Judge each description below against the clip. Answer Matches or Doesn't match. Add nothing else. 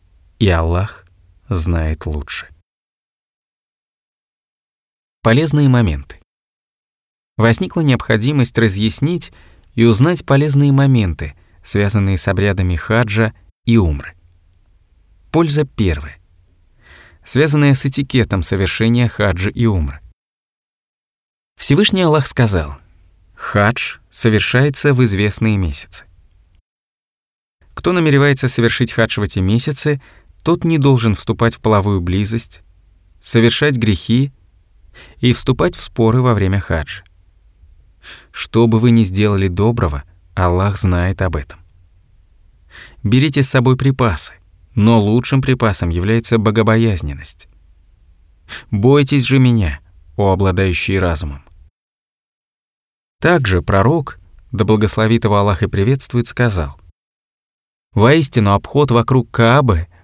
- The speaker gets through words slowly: Matches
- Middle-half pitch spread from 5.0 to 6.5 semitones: Matches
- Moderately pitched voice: Doesn't match